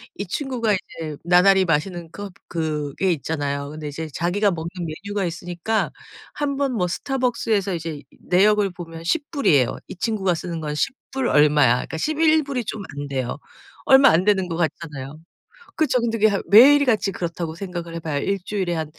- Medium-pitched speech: Yes, medium, 180 Hz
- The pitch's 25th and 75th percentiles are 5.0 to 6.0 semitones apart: Yes, average, 5.3 semitones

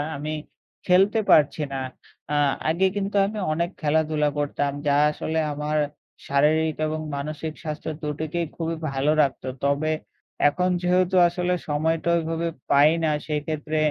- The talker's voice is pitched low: No, medium, 155 Hz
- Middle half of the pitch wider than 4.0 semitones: No, narrow, 2.4 semitones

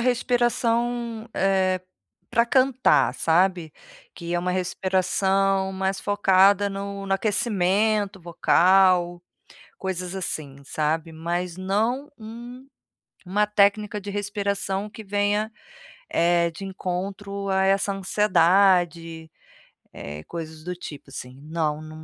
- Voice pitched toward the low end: No, high, 190 Hz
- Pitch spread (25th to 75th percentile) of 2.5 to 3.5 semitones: Yes, average, 2.8 semitones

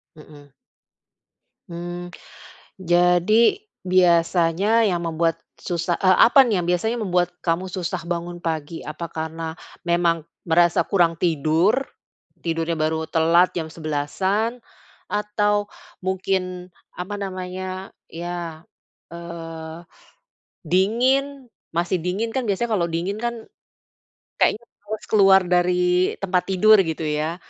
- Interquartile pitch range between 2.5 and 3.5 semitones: Yes, average, 2.8 semitones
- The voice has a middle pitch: Yes, medium, 175 Hz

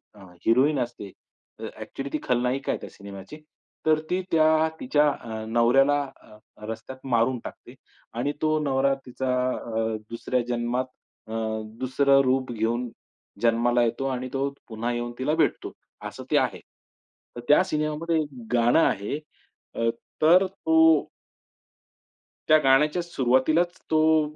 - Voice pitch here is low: Yes, low, 130 Hz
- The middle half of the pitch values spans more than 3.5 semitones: Yes, average, 4.4 semitones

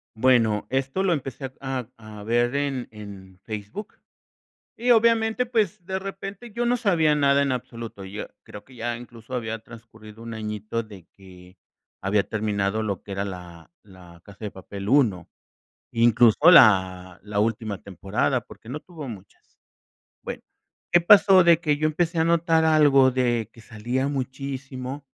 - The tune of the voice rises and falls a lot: Yes, wide, 6.2 semitones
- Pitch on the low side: Yes, low, 120 Hz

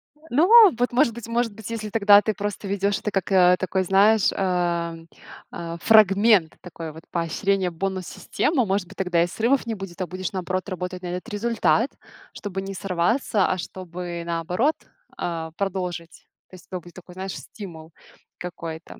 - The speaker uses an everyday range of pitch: Yes, average, 3.1 semitones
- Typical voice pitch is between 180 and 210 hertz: Yes, high, 190 Hz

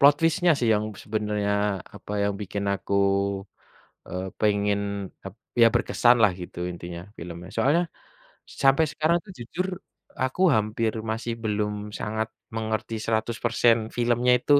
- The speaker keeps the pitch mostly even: No, average, 3.0 semitones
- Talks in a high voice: No, low, 110 Hz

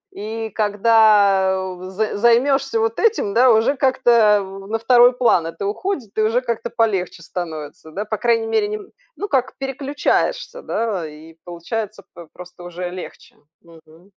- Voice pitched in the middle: No, high, 215 Hz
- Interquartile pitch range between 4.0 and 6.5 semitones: Yes, average, 4.5 semitones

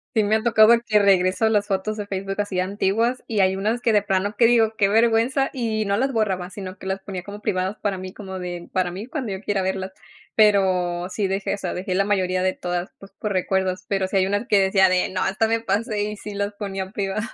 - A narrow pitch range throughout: Yes, narrow, 2.2 semitones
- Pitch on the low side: No, high, 200 Hz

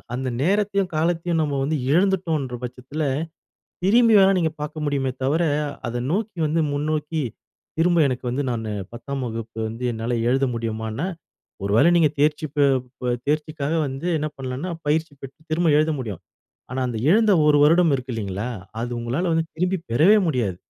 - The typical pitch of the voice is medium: Yes, medium, 150 Hz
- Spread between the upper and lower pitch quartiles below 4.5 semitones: No, average, 5.1 semitones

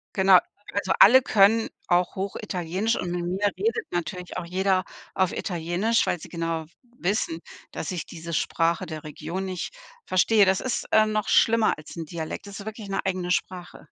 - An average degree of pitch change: Yes, average, 3.0 semitones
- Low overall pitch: No, medium, 185 Hz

